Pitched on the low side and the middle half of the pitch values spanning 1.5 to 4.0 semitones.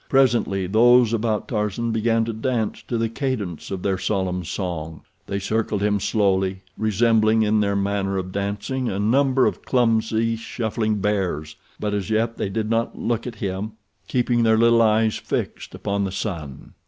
Yes: low, 110 Hz; average, 2.8 semitones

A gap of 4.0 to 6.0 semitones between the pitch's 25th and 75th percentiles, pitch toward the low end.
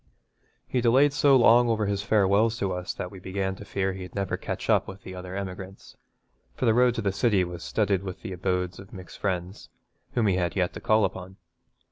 No: average, 3.0 semitones; very low, 95 Hz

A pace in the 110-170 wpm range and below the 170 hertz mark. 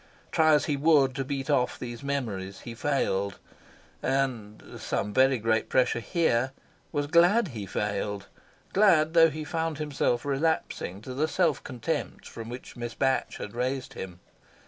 Yes: average, 155 wpm; low, 135 Hz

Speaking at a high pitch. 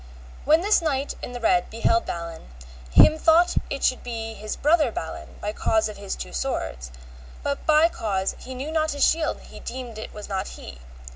Yes: high, 245 Hz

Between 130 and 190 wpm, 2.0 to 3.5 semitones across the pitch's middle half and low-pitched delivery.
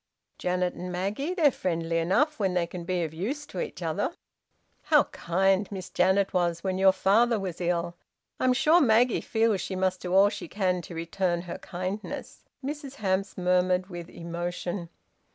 No: average, 170 wpm; average, 2.9 semitones; medium, 185 Hz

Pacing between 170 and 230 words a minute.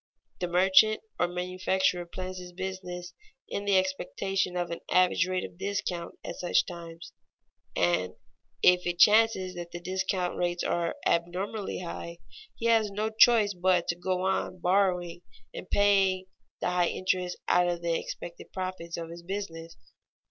No: average, 155 wpm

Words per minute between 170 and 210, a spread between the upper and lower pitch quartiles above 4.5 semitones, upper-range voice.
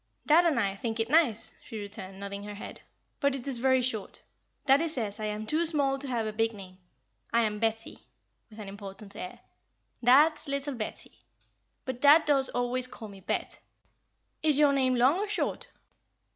Yes: average, 185 wpm; average, 4.9 semitones; high, 245 Hz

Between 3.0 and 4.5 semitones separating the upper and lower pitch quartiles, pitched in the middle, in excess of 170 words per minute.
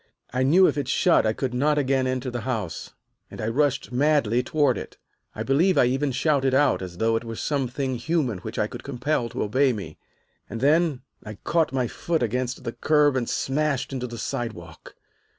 No: average, 3.6 semitones; low, 130 Hz; average, 200 wpm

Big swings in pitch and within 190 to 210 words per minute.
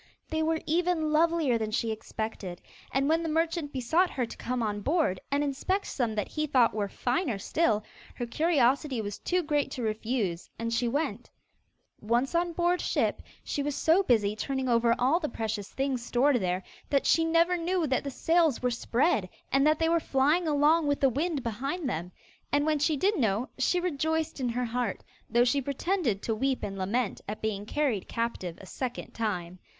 Yes: wide, 5.8 semitones; average, 195 wpm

